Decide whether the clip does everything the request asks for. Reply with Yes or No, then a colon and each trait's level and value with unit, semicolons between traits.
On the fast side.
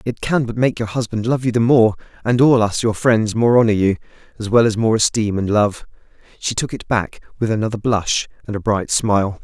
Yes: fast, 225 wpm